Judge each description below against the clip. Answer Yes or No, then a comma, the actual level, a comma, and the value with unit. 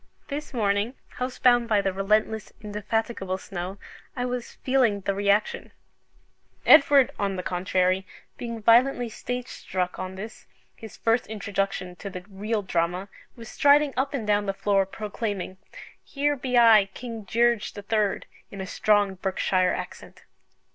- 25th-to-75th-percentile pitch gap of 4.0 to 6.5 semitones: No, average, 3.6 semitones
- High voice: Yes, high, 210 Hz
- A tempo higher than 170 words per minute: No, average, 145 wpm